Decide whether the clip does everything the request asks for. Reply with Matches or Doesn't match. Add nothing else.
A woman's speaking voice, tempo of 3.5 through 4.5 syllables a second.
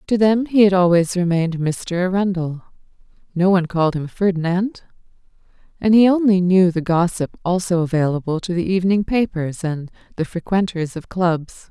Doesn't match